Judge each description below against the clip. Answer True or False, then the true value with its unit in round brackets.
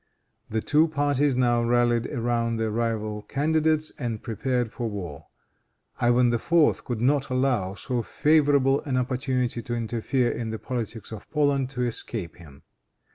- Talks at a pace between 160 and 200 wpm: False (145 wpm)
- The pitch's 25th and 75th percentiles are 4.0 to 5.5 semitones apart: False (3.3 semitones)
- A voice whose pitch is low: True (120 Hz)